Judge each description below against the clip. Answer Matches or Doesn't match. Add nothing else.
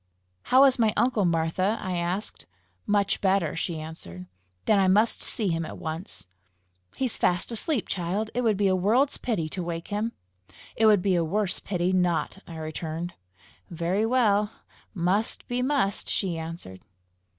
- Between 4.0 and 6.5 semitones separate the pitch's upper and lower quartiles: Matches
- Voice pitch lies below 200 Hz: Matches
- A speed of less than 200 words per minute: Matches